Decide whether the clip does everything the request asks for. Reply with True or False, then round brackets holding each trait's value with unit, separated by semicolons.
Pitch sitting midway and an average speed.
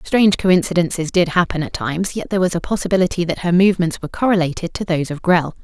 False (175 Hz; 215 wpm)